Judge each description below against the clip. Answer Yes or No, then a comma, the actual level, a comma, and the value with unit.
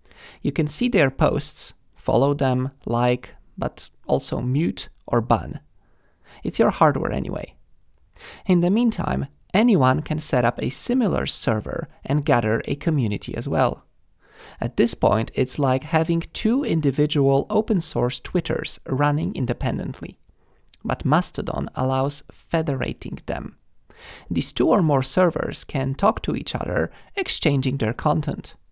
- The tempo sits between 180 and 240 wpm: No, slow, 135 wpm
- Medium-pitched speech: Yes, medium, 145 Hz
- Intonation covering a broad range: No, average, 4.4 semitones